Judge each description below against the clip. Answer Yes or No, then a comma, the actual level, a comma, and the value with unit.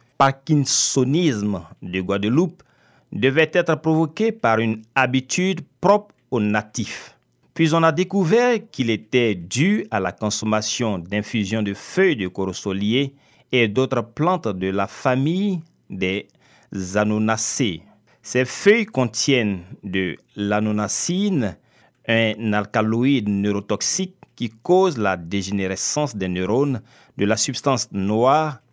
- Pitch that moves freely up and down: Yes, wide, 6.8 semitones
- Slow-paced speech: Yes, slow, 115 wpm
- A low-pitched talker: Yes, low, 120 Hz